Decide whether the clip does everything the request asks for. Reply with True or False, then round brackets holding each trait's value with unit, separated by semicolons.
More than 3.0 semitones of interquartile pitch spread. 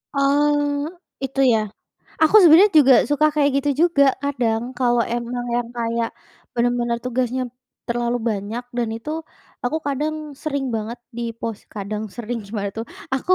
True (3.5 semitones)